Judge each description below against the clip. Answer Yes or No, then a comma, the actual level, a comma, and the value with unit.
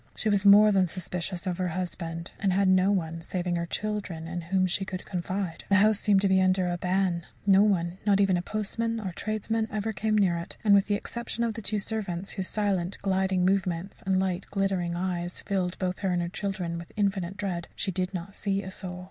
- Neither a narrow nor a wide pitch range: No, narrow, 2.2 semitones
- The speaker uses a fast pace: Yes, fast, 225 wpm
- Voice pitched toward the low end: No, high, 190 Hz